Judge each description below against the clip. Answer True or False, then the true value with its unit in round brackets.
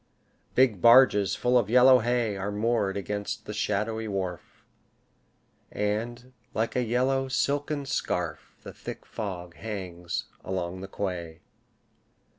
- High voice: False (105 Hz)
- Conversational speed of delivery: False (120 wpm)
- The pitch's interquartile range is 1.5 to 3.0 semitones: False (4.3 semitones)